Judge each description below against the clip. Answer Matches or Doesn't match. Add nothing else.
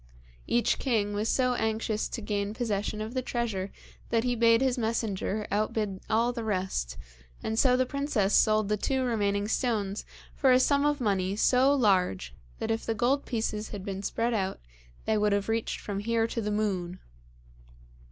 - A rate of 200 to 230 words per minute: Doesn't match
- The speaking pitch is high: Matches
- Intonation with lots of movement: Doesn't match